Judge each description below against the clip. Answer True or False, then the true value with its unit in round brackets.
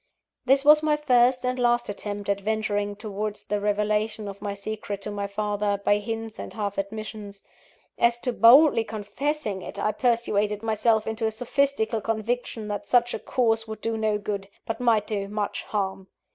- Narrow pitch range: True (2.3 semitones)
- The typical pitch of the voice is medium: False (215 Hz)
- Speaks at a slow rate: False (175 wpm)